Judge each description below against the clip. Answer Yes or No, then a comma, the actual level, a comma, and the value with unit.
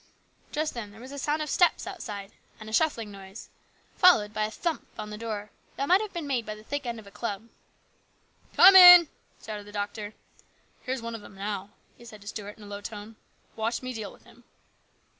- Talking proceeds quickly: Yes, fast, 235 wpm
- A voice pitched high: Yes, high, 220 Hz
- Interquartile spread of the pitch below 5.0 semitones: No, average, 5.3 semitones